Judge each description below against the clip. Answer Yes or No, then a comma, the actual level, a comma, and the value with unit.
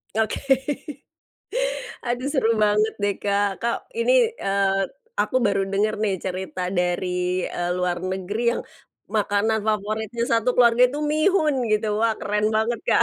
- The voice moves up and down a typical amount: Yes, average, 3.1 semitones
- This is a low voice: No, high, 215 Hz